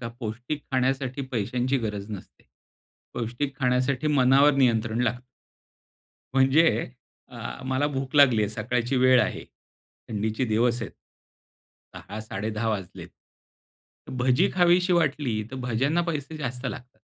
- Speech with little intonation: No, average, 3.4 semitones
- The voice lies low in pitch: Yes, low, 125 Hz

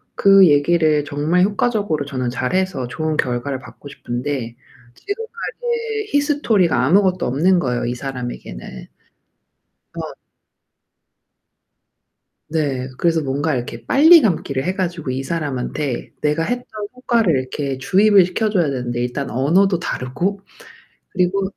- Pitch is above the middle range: No, medium, 155 Hz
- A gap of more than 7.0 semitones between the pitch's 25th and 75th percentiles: No, wide, 6.7 semitones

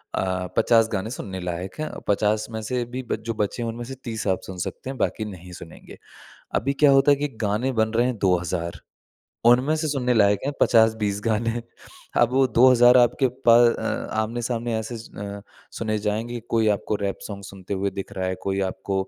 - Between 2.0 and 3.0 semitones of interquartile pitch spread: No, average, 3.4 semitones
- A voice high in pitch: No, low, 110 Hz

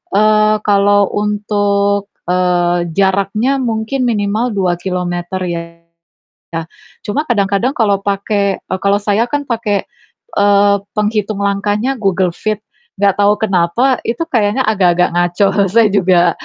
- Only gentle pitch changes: Yes, narrow, 2.1 semitones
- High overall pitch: Yes, high, 205 Hz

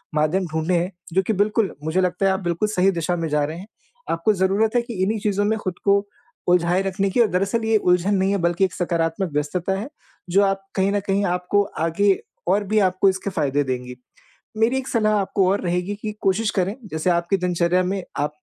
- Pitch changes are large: No, average, 2.7 semitones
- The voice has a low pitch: No, high, 190 Hz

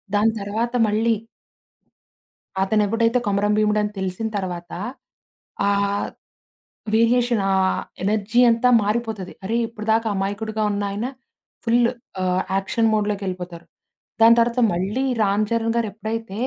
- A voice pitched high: Yes, high, 215 Hz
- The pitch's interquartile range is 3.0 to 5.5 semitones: No, narrow, 2.4 semitones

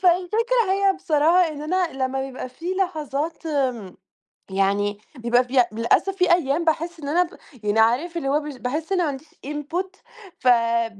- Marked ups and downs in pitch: Yes, wide, 5.9 semitones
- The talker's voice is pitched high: Yes, very high, 295 Hz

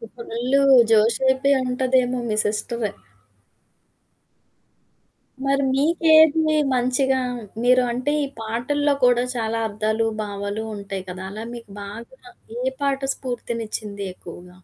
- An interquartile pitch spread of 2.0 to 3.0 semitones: No, average, 3.8 semitones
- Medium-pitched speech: No, high, 240 Hz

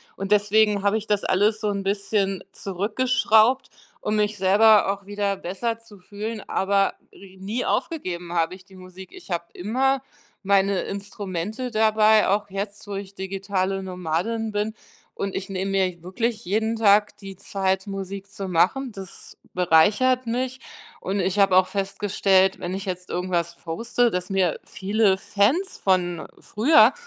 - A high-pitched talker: Yes, high, 200 Hz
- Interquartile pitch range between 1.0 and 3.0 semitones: Yes, narrow, 2.4 semitones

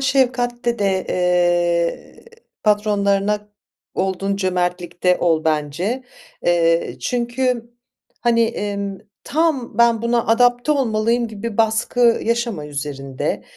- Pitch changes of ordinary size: Yes, average, 5.0 semitones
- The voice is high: Yes, high, 210 Hz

